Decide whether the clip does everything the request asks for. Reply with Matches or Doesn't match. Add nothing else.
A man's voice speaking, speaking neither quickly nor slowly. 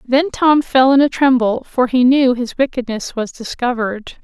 Doesn't match